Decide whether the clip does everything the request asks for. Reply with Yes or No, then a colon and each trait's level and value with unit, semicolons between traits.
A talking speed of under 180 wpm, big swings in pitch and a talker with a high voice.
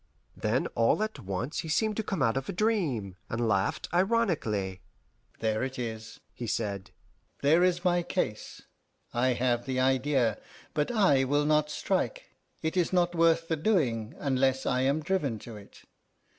No: average, 165 wpm; wide, 7.3 semitones; low, 135 Hz